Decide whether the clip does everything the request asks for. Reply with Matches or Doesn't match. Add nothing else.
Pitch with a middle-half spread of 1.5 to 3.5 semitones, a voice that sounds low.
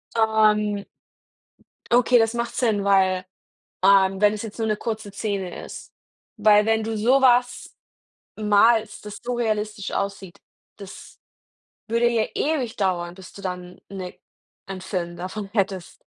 Doesn't match